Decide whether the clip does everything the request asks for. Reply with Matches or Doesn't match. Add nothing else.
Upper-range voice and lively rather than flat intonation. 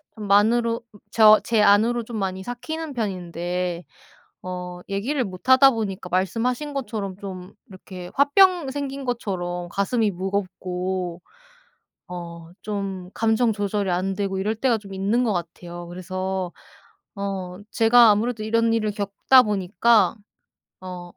Doesn't match